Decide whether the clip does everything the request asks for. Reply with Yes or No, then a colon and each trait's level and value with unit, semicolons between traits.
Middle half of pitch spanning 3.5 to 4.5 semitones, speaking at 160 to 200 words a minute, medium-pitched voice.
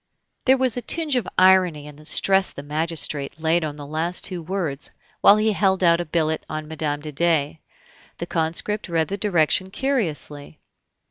Yes: average, 3.9 semitones; average, 180 wpm; medium, 170 Hz